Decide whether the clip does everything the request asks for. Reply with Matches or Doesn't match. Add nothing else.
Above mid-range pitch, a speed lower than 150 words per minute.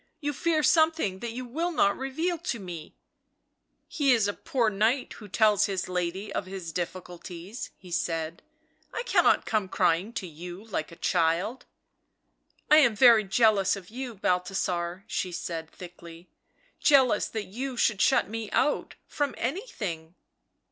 Doesn't match